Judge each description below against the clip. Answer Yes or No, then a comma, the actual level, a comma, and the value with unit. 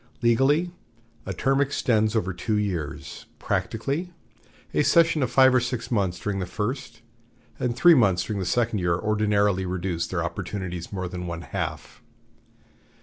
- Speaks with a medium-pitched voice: No, low, 105 Hz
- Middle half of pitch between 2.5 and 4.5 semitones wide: No, wide, 5.6 semitones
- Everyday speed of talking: Yes, average, 150 wpm